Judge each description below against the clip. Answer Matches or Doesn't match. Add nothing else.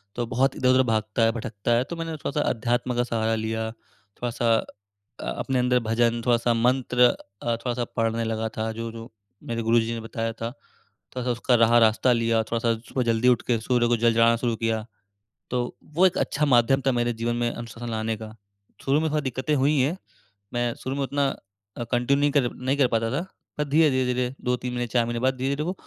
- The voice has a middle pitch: Doesn't match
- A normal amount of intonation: Doesn't match